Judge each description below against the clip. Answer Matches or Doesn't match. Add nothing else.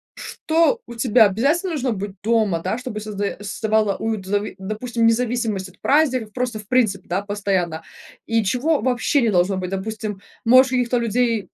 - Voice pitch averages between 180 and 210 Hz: Doesn't match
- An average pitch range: Matches